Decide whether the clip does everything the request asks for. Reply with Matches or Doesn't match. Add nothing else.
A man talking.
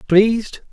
Matches